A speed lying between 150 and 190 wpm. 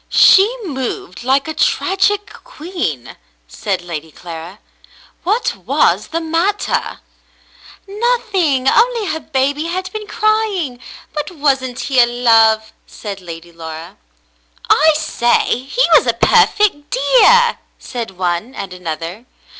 No: slow, 135 wpm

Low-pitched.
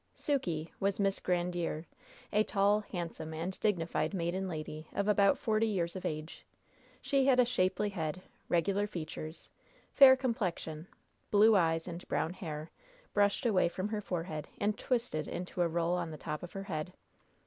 No: medium, 180 Hz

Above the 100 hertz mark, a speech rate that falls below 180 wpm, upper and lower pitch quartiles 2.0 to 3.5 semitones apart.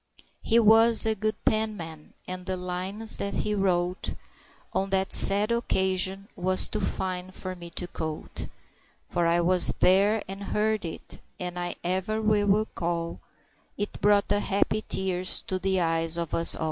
Yes: high, 190 Hz; average, 160 wpm; average, 2.7 semitones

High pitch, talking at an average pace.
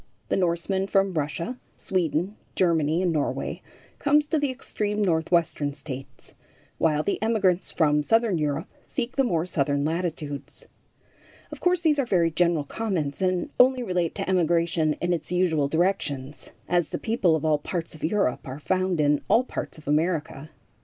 No: medium, 170 Hz; average, 160 wpm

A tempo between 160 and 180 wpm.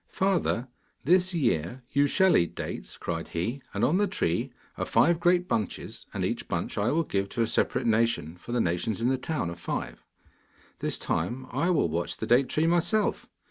No: average, 195 wpm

